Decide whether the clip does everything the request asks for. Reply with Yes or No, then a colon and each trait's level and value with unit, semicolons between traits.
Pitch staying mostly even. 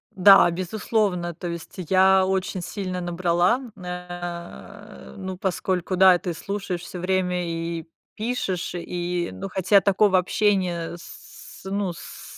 Yes: narrow, 1.8 semitones